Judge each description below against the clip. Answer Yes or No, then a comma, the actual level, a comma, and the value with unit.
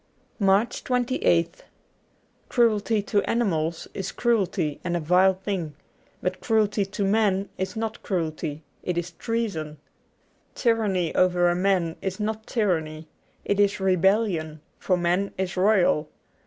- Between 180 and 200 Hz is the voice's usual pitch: Yes, high, 190 Hz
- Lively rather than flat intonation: No, average, 3.6 semitones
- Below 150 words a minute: Yes, slow, 135 wpm